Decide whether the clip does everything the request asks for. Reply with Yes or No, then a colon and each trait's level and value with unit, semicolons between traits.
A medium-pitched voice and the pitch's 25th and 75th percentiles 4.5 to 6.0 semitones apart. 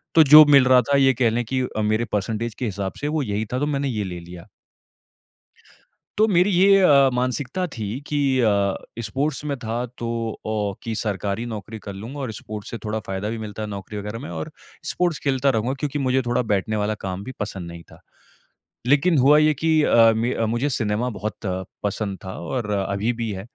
No: low, 115 Hz; average, 4.8 semitones